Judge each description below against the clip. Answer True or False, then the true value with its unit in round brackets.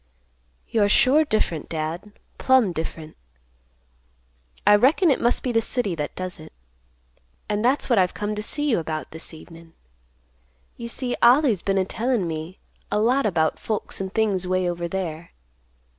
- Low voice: False (200 Hz)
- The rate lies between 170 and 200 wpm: False (160 wpm)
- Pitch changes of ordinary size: False (5.9 semitones)